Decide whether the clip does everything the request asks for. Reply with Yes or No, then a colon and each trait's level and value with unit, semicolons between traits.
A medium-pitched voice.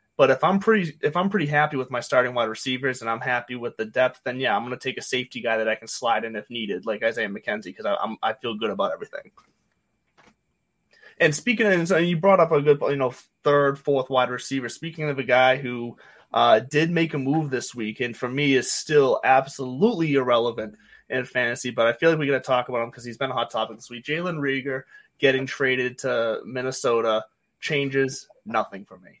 No: low, 130 Hz